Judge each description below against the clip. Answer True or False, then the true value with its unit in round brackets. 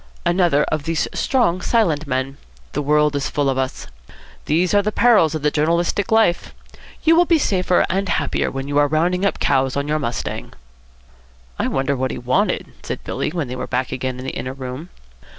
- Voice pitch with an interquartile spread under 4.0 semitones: False (5.1 semitones)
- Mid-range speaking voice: True (150 Hz)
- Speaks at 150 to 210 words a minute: True (200 wpm)